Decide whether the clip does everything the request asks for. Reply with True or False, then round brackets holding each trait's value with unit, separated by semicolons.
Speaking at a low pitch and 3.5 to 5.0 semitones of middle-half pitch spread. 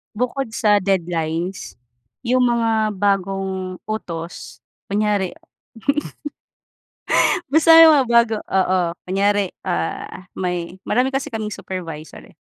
False (200 Hz; 4.0 semitones)